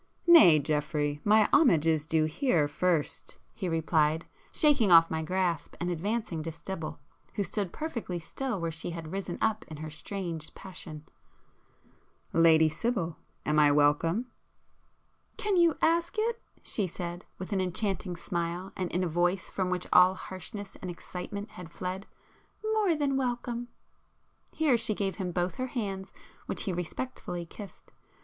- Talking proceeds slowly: No, average, 150 wpm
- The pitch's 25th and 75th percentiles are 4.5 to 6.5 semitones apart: Yes, average, 4.8 semitones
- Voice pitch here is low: No, medium, 180 Hz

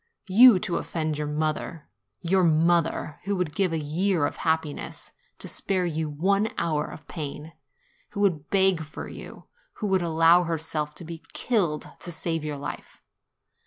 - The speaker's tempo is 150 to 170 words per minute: Yes, average, 165 wpm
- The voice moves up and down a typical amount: Yes, average, 3.2 semitones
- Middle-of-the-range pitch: Yes, medium, 165 Hz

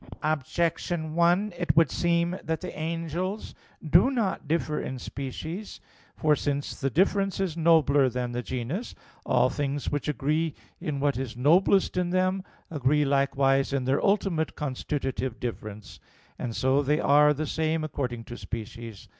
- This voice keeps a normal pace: Yes, average, 150 wpm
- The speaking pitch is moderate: Yes, medium, 150 Hz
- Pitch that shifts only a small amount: No, average, 4.1 semitones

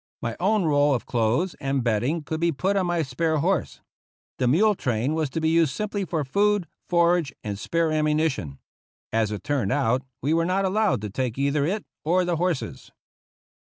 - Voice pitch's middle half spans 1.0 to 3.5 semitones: No, average, 5.2 semitones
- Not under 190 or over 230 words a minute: Yes, average, 195 wpm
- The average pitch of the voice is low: No, medium, 155 Hz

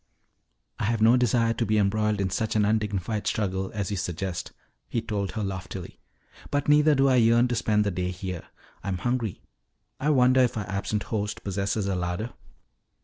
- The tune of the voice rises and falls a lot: No, average, 3.2 semitones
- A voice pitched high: No, low, 105 Hz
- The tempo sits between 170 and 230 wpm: Yes, average, 185 wpm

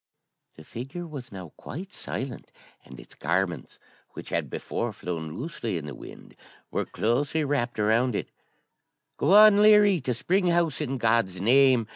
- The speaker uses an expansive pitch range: Yes, wide, 7.6 semitones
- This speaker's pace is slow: No, average, 155 wpm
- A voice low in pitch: Yes, low, 125 Hz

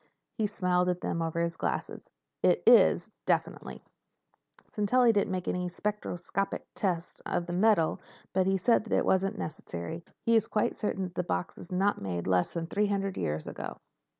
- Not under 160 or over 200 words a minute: Yes, average, 170 wpm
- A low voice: No, medium, 180 Hz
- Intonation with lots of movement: No, average, 3.6 semitones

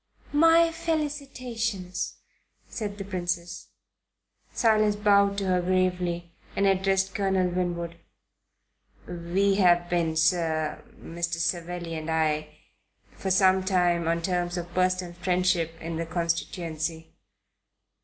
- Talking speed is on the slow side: Yes, slow, 115 wpm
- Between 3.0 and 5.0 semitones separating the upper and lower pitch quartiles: No, narrow, 2.5 semitones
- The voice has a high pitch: No, medium, 180 Hz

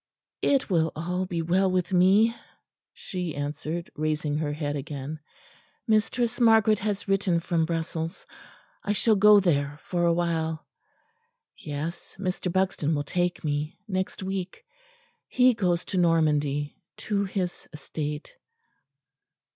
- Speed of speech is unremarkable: No, slow, 125 wpm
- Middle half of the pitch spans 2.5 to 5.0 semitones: Yes, average, 3.8 semitones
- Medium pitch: Yes, medium, 175 Hz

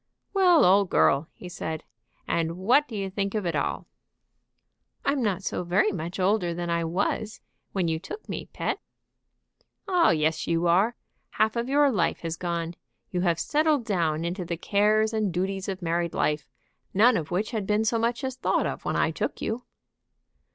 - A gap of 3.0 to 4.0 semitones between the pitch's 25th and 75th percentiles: No, average, 4.6 semitones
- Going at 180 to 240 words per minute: Yes, average, 185 wpm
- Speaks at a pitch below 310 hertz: Yes, high, 190 Hz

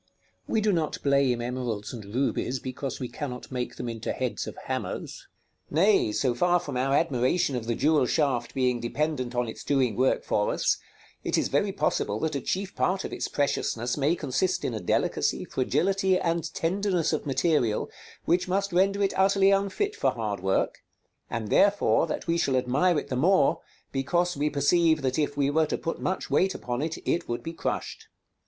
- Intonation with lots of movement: Yes, wide, 6.0 semitones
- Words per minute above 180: Yes, average, 190 wpm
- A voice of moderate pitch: Yes, medium, 145 Hz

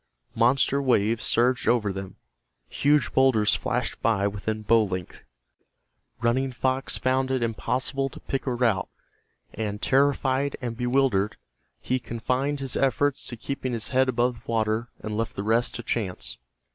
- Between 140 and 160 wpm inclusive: Yes, average, 150 wpm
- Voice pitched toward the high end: No, low, 120 Hz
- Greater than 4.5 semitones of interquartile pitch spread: No, average, 3.3 semitones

